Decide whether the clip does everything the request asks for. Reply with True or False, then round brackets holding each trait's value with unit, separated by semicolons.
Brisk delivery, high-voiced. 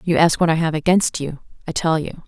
False (265 wpm; 160 Hz)